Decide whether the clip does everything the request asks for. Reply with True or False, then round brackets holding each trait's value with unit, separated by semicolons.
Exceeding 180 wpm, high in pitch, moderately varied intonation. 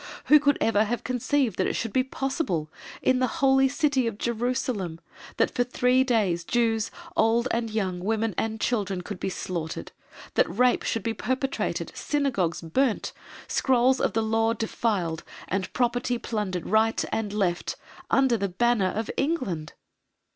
False (155 wpm; 225 Hz; 4.4 semitones)